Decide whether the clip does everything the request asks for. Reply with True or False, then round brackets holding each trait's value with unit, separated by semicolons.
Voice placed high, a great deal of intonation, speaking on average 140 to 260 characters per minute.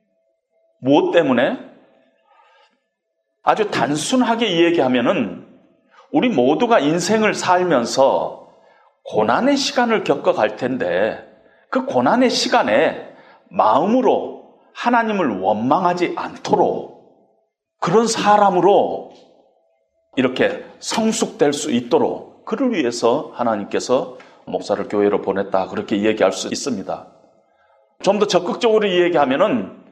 True (215 Hz; 6.1 semitones; 240 characters per minute)